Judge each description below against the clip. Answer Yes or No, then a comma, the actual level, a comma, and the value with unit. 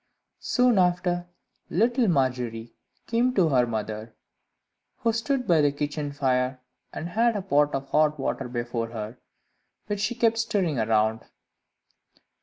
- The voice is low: No, medium, 150 Hz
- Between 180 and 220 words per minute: No, slow, 135 wpm